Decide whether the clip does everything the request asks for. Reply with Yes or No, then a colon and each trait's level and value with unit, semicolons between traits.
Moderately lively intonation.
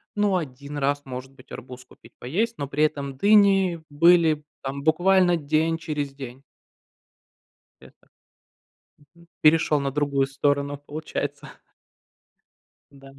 Yes: average, 3.0 semitones